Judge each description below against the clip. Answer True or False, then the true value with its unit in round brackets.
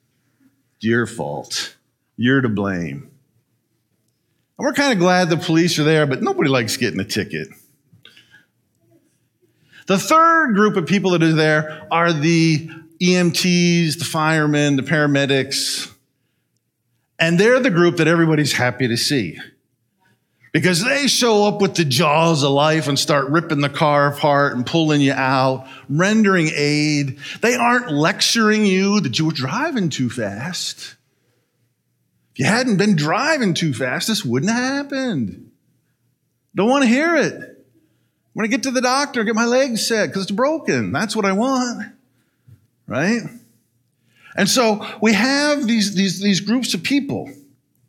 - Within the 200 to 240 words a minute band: False (150 wpm)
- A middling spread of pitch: False (7.8 semitones)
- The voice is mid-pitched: True (165 Hz)